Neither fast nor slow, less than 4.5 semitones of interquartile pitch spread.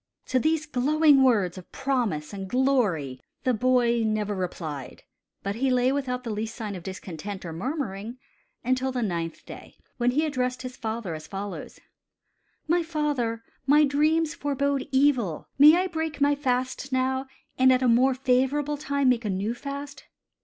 No: average, 165 wpm; average, 5.0 semitones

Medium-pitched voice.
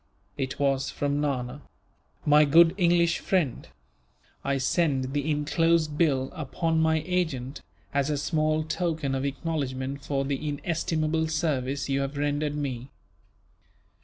Yes: medium, 145 Hz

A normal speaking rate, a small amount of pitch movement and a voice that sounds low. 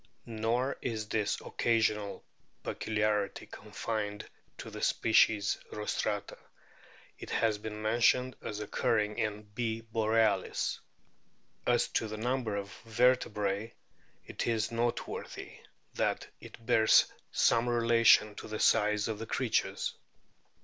No: slow, 115 wpm; narrow, 1.6 semitones; low, 110 Hz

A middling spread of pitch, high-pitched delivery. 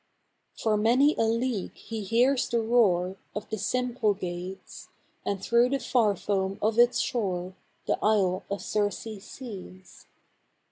Yes: average, 3.8 semitones; high, 215 Hz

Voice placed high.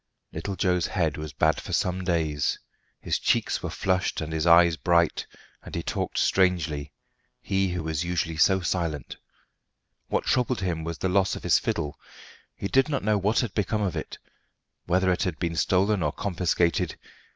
No: very low, 90 Hz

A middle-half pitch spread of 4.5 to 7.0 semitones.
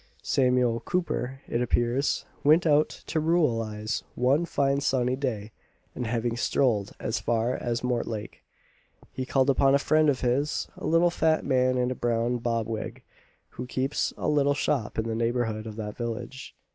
No: average, 3.2 semitones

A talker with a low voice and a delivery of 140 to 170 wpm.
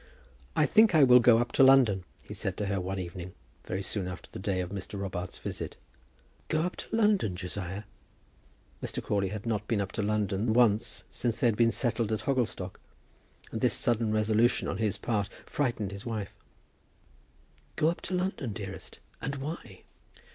No: low, 110 Hz; average, 180 wpm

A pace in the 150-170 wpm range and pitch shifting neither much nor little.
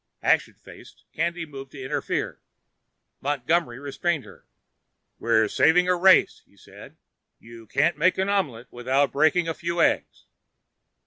No: slow, 135 wpm; average, 4.7 semitones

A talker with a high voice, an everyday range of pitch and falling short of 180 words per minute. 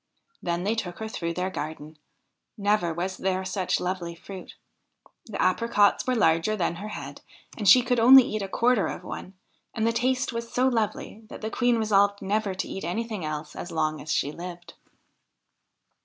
No: high, 195 Hz; average, 4.5 semitones; average, 185 wpm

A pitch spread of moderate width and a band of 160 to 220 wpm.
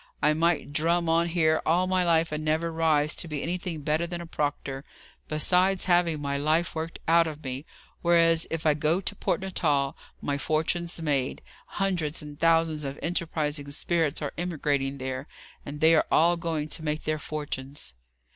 No: narrow, 2.3 semitones; average, 180 wpm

